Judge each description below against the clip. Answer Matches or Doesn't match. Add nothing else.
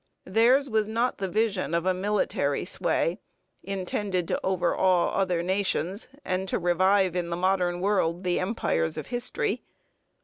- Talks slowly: Doesn't match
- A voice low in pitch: Doesn't match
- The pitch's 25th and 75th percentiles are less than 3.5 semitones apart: Matches